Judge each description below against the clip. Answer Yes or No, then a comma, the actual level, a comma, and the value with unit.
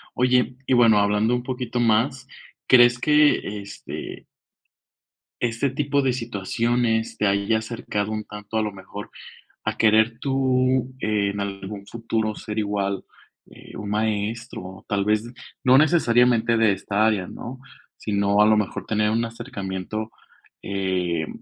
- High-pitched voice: No, low, 110 Hz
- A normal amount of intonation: Yes, average, 3.0 semitones